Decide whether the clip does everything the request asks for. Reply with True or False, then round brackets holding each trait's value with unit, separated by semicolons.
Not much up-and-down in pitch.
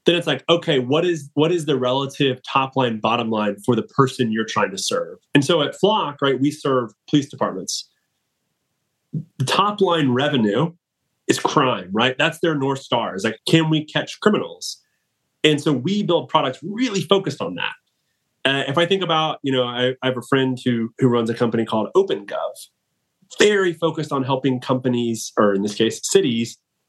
False (4.9 semitones)